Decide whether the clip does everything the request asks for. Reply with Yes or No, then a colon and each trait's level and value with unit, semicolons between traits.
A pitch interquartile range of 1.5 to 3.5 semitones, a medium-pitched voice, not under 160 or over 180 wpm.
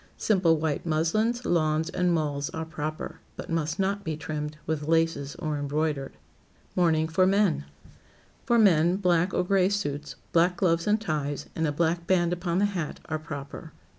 Yes: average, 2.9 semitones; medium, 165 Hz; average, 170 wpm